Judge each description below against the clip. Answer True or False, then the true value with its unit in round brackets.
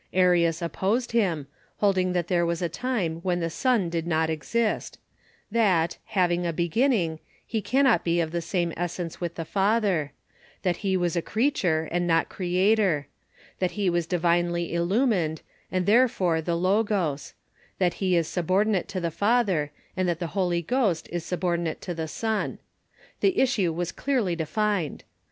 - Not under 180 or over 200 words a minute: False (165 wpm)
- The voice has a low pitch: False (175 Hz)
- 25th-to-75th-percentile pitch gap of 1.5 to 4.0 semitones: True (3.4 semitones)